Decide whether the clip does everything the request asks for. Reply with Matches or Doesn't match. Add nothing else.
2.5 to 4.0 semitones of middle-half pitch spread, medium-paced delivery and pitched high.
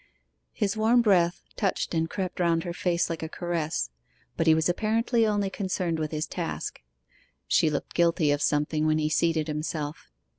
Doesn't match